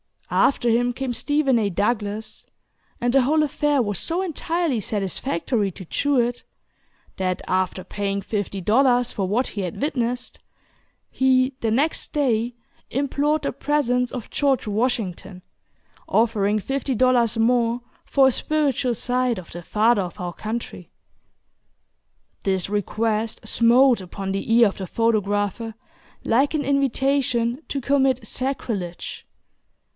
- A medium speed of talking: No, slow, 130 wpm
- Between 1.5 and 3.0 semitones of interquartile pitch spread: No, average, 4.5 semitones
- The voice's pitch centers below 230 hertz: No, high, 235 Hz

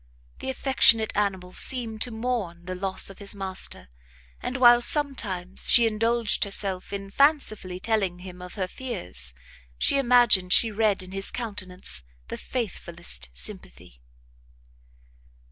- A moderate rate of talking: No, slow, 130 wpm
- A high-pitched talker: Yes, high, 200 Hz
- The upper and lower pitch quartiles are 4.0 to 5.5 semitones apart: Yes, average, 4.5 semitones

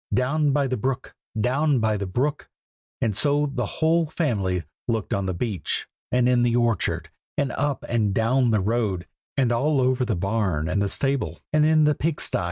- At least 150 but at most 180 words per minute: No, average, 190 wpm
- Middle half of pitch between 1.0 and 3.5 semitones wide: No, average, 5.3 semitones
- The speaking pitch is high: No, low, 125 Hz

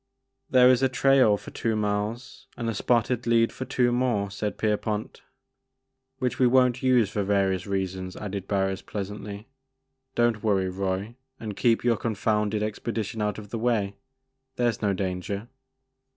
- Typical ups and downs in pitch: Yes, average, 3.0 semitones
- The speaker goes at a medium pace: Yes, average, 160 wpm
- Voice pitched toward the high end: No, low, 105 Hz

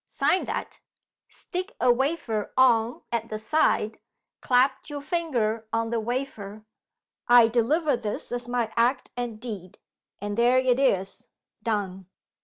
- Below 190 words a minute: Yes, slow, 135 wpm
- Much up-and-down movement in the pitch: No, average, 3.0 semitones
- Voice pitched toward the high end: Yes, high, 235 Hz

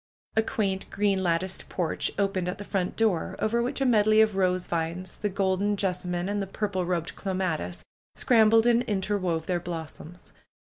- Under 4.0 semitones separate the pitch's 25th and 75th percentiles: Yes, average, 2.7 semitones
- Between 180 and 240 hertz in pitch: Yes, high, 190 Hz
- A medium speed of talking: Yes, average, 175 wpm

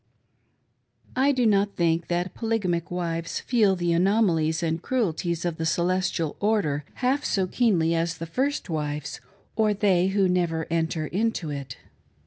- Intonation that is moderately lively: Yes, average, 4.1 semitones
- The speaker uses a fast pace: No, average, 155 wpm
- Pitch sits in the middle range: Yes, medium, 175 Hz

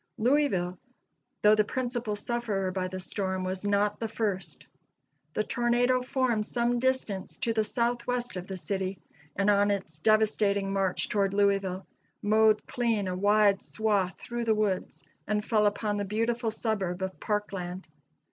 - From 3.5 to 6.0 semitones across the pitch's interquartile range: No, average, 2.9 semitones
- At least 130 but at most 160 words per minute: Yes, average, 150 wpm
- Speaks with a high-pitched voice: Yes, high, 210 Hz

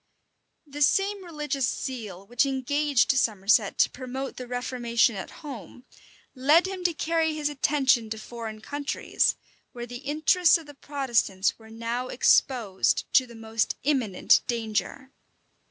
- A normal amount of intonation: Yes, average, 4.3 semitones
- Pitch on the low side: No, very high, 255 Hz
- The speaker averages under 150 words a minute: Yes, average, 140 wpm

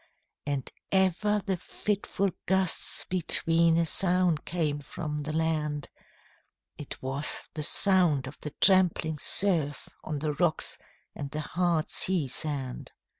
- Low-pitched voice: No, medium, 160 Hz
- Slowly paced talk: Yes, slow, 125 wpm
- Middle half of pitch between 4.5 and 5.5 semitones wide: No, average, 3.7 semitones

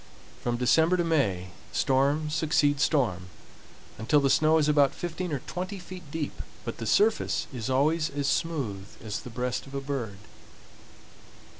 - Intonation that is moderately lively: Yes, average, 4.5 semitones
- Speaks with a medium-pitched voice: Yes, medium, 145 Hz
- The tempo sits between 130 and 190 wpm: Yes, average, 155 wpm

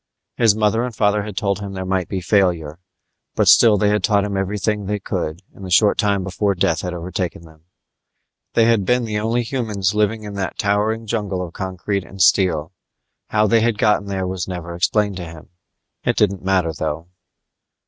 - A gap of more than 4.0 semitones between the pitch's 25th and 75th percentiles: No, narrow, 2.5 semitones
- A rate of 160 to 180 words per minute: No, average, 195 wpm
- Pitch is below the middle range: Yes, low, 100 Hz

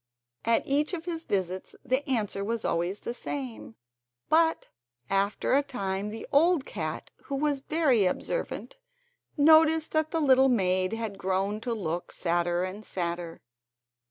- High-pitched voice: Yes, high, 220 Hz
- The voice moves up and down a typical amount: No, wide, 7.5 semitones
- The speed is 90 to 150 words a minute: Yes, average, 145 wpm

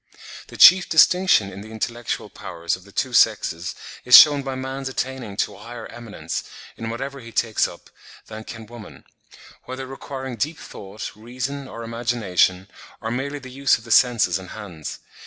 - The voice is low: Yes, low, 120 Hz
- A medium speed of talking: Yes, average, 170 wpm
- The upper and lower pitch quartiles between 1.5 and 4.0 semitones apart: Yes, average, 3.6 semitones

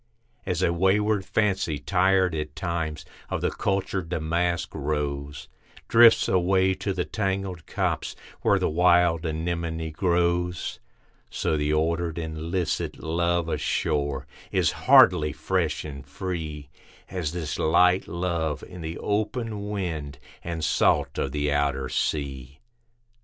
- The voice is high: No, very low, 85 Hz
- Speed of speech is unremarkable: No, slow, 125 wpm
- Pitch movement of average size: Yes, average, 3.3 semitones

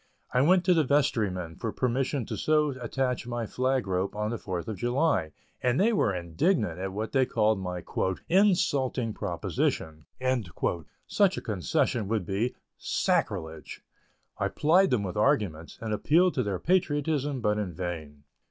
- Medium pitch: No, low, 115 Hz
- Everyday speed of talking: Yes, average, 155 wpm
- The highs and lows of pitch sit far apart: Yes, wide, 7.0 semitones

